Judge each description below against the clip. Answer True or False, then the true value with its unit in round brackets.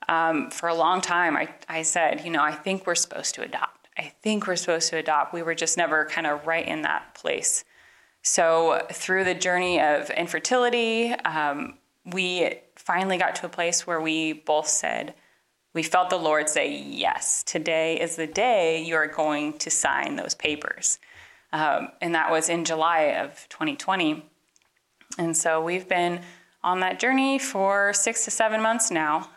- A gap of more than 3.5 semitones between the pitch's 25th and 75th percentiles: False (3.0 semitones)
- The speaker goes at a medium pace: True (180 wpm)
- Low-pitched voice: False (170 Hz)